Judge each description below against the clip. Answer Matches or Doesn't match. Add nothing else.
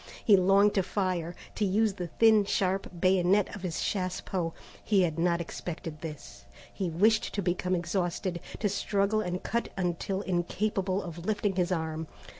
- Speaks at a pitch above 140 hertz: Matches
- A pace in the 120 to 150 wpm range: Doesn't match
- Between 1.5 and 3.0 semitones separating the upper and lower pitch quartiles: Matches